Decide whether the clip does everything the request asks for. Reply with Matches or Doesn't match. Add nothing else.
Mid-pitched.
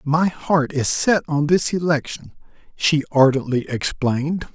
Matches